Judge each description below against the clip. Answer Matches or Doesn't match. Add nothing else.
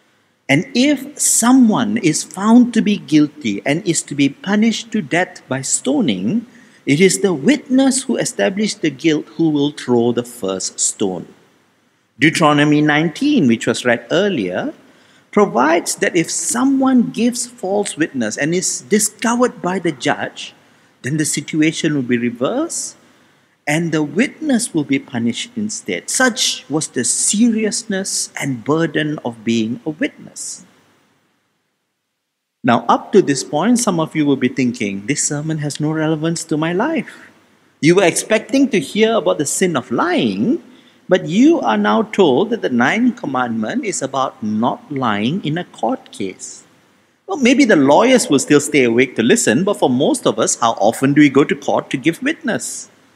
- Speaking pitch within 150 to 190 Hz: Matches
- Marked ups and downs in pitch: Matches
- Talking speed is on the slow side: Doesn't match